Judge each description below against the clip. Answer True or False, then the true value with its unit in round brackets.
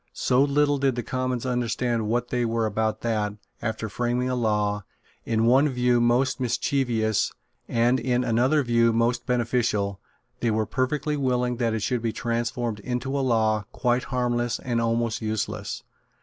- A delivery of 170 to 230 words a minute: False (160 wpm)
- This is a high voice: False (120 Hz)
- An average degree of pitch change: False (2.1 semitones)